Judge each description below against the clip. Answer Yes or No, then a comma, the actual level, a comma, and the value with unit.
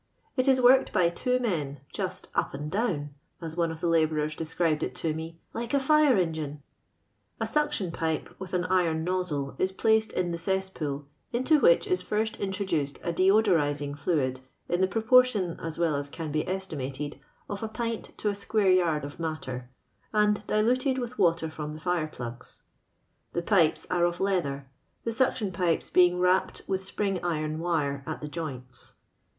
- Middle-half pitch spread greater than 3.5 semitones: Yes, average, 5.1 semitones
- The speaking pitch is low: No, medium, 175 Hz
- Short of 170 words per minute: No, average, 175 wpm